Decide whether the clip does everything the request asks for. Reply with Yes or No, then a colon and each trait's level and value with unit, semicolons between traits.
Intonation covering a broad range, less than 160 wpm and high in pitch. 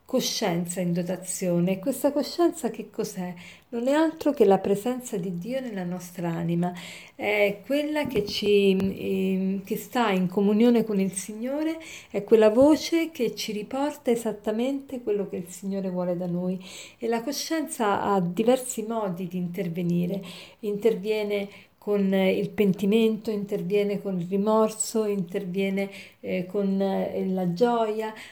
No: average, 3.3 semitones; average, 140 wpm; high, 205 Hz